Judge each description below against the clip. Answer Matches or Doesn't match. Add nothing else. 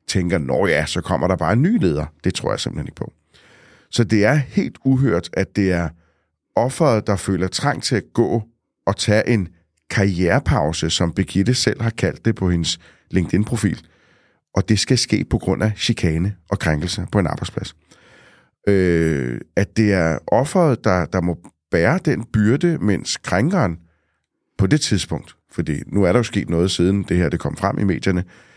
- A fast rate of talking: Doesn't match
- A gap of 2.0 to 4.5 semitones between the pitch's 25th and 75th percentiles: Doesn't match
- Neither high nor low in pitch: Doesn't match